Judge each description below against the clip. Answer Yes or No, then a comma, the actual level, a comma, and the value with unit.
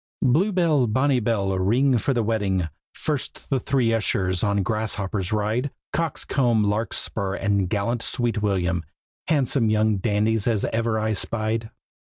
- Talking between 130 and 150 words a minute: Yes, average, 140 wpm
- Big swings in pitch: No, average, 3.3 semitones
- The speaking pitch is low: Yes, low, 110 Hz